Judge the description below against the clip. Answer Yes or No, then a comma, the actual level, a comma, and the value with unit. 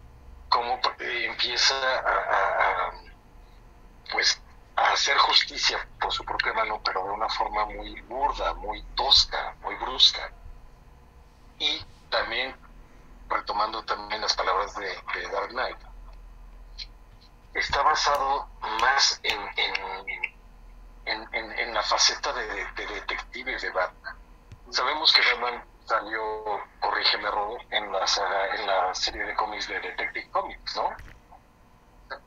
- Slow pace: Yes, slow, 115 wpm